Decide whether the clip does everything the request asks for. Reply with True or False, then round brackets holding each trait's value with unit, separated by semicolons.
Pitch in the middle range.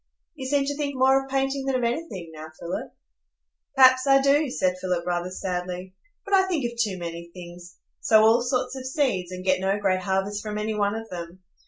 False (215 Hz)